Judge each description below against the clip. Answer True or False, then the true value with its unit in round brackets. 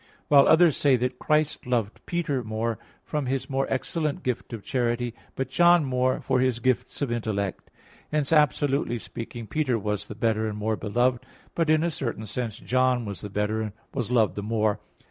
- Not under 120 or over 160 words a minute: False (185 wpm)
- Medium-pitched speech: False (125 Hz)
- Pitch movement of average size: True (4.0 semitones)